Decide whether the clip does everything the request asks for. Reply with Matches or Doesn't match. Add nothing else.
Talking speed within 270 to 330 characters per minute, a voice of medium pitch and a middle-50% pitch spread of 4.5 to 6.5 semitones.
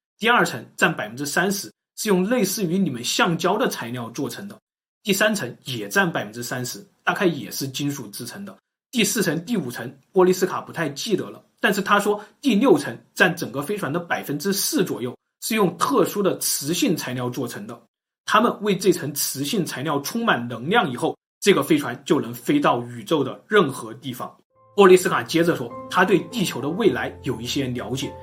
Doesn't match